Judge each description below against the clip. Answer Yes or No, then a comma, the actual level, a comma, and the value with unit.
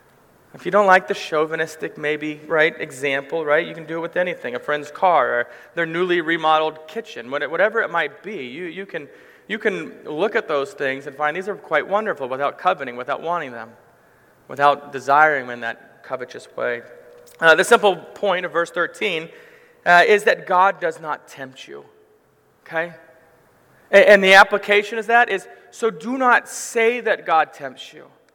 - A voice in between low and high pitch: Yes, medium, 175 Hz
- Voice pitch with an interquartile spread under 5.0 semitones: No, average, 5.3 semitones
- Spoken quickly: No, average, 180 wpm